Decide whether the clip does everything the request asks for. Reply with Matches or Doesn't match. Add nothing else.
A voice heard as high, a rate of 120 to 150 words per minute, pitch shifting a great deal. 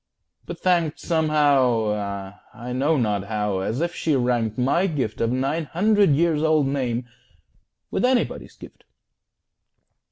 Doesn't match